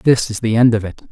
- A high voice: No, low, 115 Hz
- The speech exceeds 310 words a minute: Yes, fast, 320 wpm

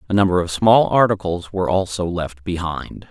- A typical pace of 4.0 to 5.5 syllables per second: Yes, 5.1 syllables/s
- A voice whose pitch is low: Yes, very low, 90 Hz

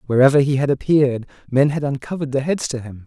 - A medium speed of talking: No, fast, 215 wpm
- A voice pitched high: No, low, 135 Hz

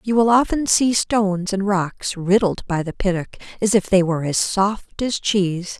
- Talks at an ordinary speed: Yes, average, 195 wpm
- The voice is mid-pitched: No, high, 195 Hz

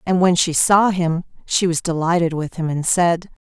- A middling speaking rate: No, fast, 210 wpm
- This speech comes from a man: No, female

